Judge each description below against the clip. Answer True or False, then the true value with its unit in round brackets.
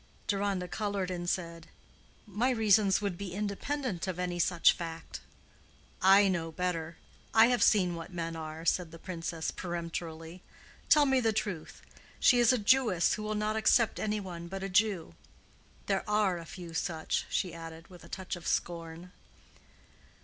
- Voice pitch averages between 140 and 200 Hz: True (185 Hz)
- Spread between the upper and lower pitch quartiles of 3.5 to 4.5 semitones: True (3.8 semitones)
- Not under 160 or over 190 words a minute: True (165 wpm)